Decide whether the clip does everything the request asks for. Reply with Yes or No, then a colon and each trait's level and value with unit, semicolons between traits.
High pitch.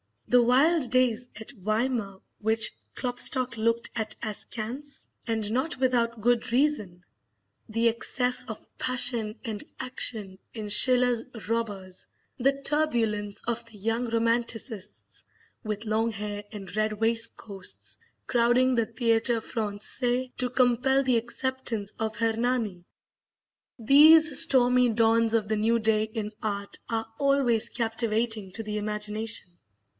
Yes: high, 230 Hz